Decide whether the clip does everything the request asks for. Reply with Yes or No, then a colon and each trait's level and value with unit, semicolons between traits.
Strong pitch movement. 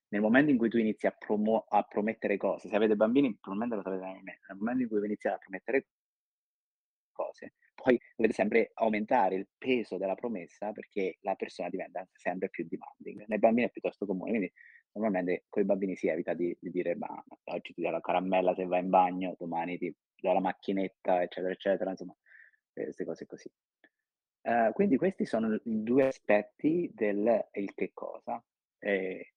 No: average, 3.6 semitones